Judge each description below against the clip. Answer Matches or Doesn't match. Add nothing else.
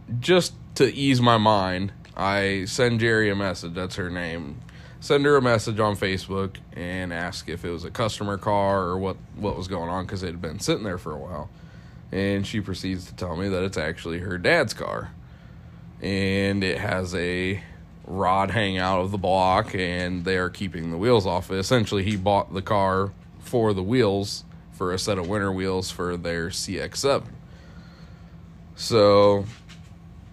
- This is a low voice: Matches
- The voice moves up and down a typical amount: Doesn't match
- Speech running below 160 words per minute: Doesn't match